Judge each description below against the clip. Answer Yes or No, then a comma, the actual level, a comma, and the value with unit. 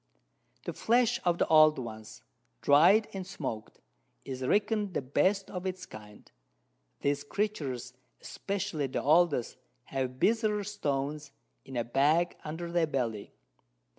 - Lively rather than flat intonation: Yes, wide, 6.6 semitones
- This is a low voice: No, medium, 155 Hz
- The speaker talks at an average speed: No, slow, 130 wpm